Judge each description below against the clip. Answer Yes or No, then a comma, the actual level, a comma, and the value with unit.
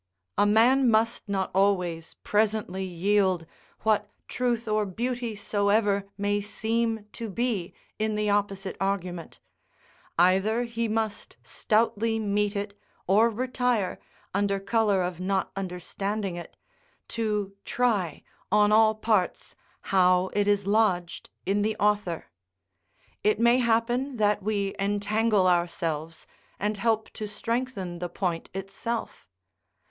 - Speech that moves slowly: Yes, slow, 120 wpm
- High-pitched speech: Yes, high, 205 Hz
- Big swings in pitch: No, narrow, 2.5 semitones